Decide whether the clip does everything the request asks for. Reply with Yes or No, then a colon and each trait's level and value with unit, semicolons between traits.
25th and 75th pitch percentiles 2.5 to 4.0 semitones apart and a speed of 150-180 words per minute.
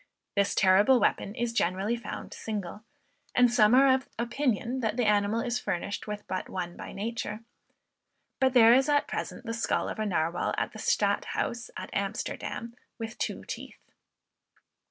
Yes: average, 3.1 semitones; average, 160 wpm